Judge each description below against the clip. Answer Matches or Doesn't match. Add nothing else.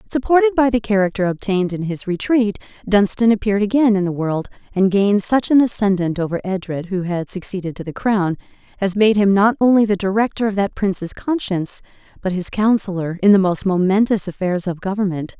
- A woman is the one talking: Matches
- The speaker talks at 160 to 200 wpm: Matches